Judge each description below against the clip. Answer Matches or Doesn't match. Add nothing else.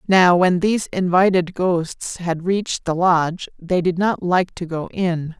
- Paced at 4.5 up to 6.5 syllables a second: Doesn't match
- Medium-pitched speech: Matches